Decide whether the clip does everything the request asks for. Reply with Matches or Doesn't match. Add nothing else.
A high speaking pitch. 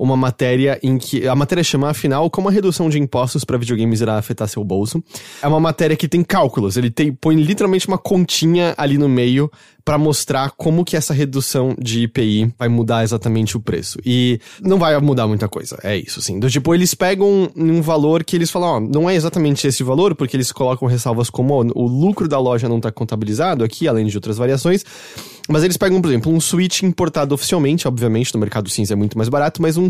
Doesn't match